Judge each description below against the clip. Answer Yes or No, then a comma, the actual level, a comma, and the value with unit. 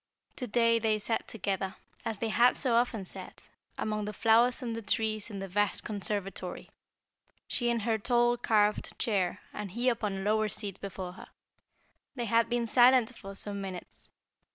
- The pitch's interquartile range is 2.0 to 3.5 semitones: Yes, average, 2.8 semitones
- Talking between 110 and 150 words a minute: No, average, 175 wpm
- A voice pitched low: No, high, 215 Hz